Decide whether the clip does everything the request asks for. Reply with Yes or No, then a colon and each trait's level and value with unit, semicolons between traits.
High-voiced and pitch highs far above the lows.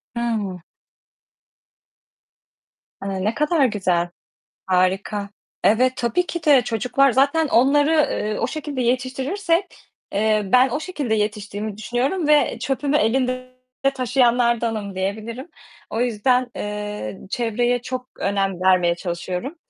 No: high, 235 Hz; average, 4.4 semitones